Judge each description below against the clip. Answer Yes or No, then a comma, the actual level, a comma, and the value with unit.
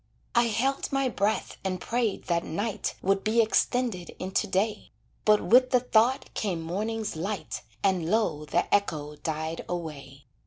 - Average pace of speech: Yes, average, 150 wpm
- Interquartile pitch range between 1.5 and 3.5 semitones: No, average, 5.1 semitones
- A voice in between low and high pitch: No, high, 200 Hz